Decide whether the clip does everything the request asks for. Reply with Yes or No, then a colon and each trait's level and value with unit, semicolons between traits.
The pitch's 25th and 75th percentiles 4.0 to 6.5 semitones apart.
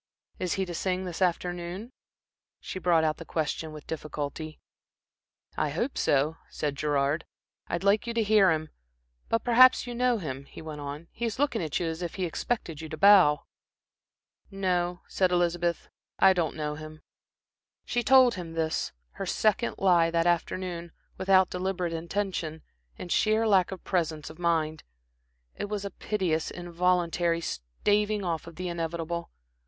No: average, 3.3 semitones